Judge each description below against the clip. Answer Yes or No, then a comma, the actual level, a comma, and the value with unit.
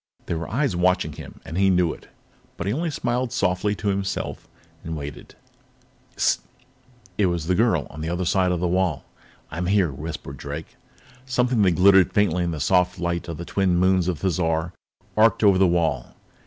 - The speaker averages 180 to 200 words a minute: Yes, average, 190 wpm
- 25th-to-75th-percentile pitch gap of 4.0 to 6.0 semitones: No, average, 3.0 semitones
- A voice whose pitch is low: Yes, very low, 90 Hz